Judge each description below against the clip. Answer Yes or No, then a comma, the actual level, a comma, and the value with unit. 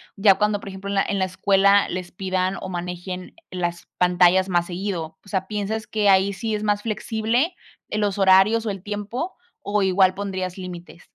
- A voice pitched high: Yes, high, 195 Hz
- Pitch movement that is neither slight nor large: No, narrow, 2.1 semitones